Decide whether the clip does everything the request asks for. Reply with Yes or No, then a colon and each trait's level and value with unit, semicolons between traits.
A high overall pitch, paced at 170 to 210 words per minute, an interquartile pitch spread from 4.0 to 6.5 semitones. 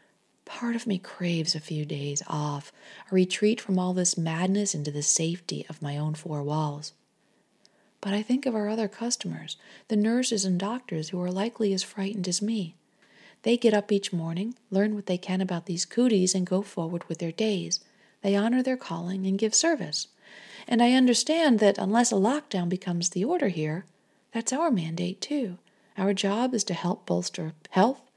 Yes: high, 195 Hz; average, 185 wpm; average, 4.4 semitones